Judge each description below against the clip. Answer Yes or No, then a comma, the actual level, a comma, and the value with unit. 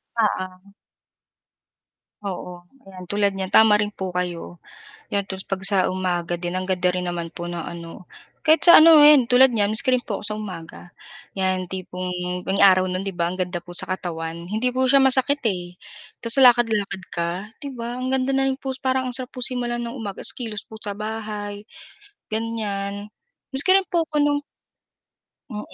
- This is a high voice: Yes, high, 205 Hz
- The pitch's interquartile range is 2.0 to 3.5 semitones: No, wide, 5.4 semitones